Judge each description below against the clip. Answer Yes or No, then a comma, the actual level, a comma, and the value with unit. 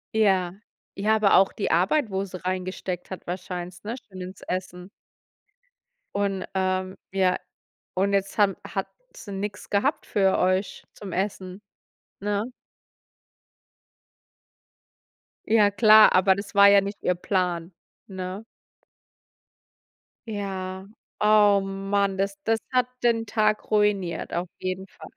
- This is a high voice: Yes, high, 195 Hz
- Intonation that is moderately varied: No, narrow, 1.8 semitones